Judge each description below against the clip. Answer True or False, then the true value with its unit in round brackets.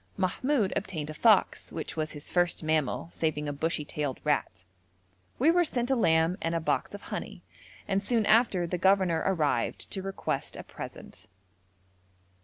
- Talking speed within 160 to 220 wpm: True (165 wpm)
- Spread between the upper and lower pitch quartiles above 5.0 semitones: False (4.4 semitones)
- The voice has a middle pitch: True (175 Hz)